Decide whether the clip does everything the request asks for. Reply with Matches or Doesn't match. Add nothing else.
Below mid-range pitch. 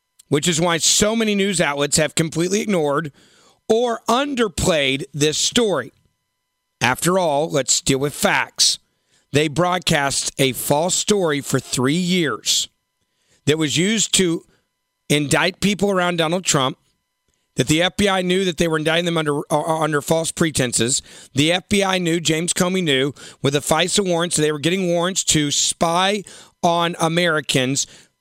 Doesn't match